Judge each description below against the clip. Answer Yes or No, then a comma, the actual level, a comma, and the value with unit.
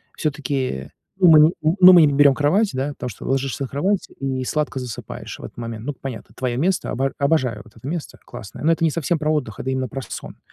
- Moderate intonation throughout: Yes, average, 3.5 semitones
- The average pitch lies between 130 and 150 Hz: Yes, medium, 140 Hz